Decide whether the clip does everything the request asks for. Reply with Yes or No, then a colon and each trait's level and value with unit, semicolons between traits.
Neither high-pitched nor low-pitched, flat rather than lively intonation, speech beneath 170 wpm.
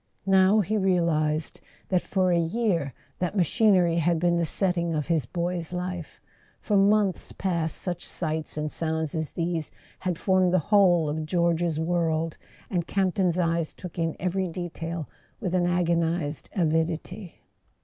Yes: medium, 170 Hz; narrow, 2.2 semitones; average, 150 wpm